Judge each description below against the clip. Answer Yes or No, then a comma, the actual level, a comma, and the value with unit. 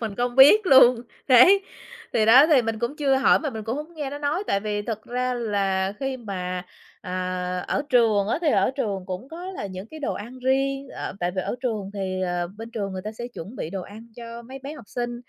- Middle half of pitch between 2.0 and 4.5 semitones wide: No, average, 5.2 semitones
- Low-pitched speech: No, high, 235 Hz